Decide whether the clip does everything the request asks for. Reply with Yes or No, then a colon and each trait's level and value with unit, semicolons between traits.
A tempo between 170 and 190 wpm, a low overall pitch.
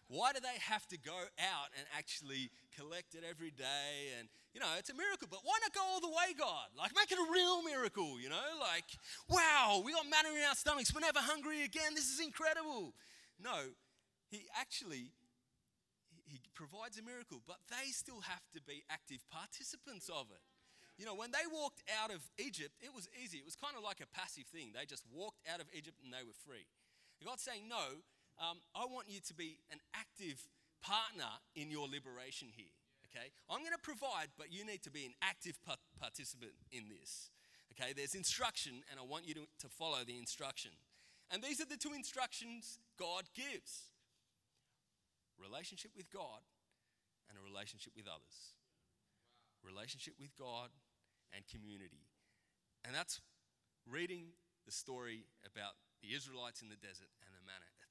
No: average, 180 wpm; medium, 170 Hz